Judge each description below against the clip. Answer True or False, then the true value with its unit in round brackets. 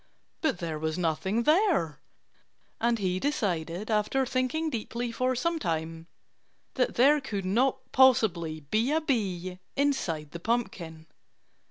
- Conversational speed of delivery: False (130 wpm)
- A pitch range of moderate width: False (7.6 semitones)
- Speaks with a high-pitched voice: True (220 Hz)